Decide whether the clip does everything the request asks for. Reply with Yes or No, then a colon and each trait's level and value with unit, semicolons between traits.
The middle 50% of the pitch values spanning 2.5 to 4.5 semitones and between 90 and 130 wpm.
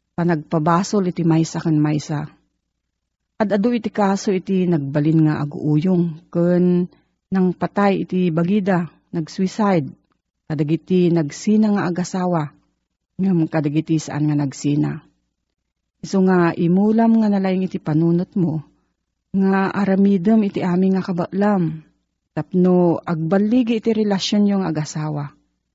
Yes: average, 3.7 semitones; slow, 110 wpm